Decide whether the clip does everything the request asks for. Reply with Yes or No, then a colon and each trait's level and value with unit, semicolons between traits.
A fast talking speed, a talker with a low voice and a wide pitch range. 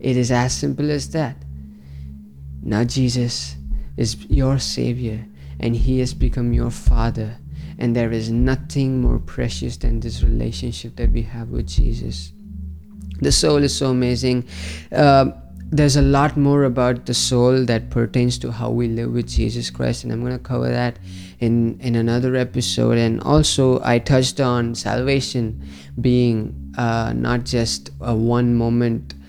No: average, 155 wpm; low, 120 Hz; wide, 7.1 semitones